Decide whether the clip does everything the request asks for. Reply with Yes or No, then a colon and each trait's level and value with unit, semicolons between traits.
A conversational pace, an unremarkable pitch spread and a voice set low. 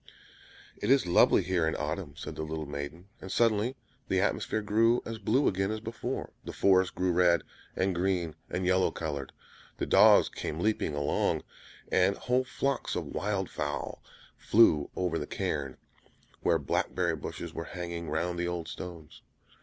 Yes: average, 160 wpm; average, 4.0 semitones; very low, 90 Hz